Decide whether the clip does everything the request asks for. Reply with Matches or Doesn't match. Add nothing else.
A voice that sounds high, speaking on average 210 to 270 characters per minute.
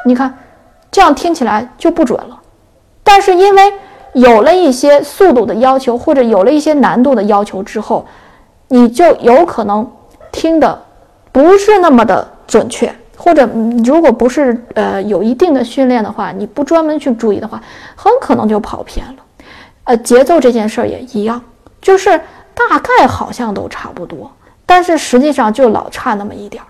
Matches